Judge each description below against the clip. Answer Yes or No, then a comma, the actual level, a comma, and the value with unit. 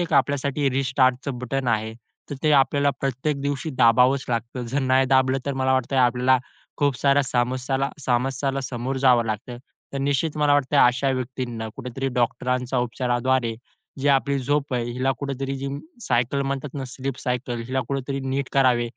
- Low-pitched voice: Yes, low, 130 Hz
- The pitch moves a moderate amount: No, narrow, 1.8 semitones